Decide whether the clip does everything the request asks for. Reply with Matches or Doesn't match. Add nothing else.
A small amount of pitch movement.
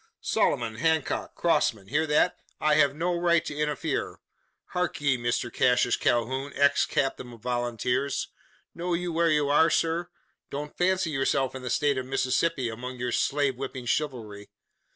Doesn't match